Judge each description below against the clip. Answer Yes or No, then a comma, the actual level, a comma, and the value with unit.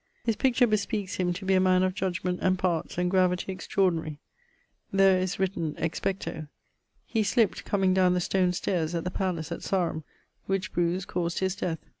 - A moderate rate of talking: Yes, average, 180 wpm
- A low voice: No, medium, 185 Hz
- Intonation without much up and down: Yes, narrow, 1.6 semitones